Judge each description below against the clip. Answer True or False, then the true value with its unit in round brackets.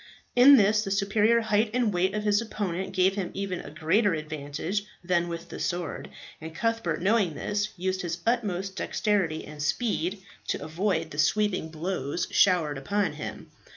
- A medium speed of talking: True (165 wpm)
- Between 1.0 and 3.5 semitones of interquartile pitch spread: False (4.1 semitones)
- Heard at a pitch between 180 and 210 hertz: True (190 Hz)